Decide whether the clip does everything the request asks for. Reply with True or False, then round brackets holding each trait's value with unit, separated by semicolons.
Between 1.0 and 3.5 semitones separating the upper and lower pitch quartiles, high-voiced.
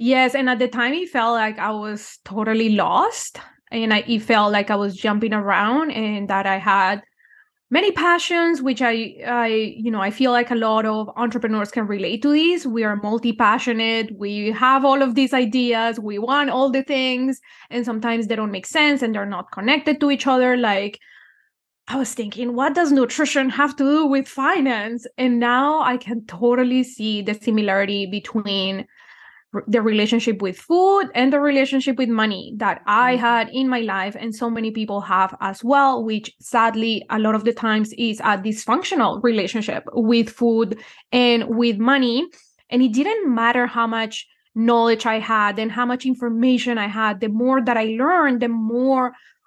True (3.2 semitones; 235 Hz)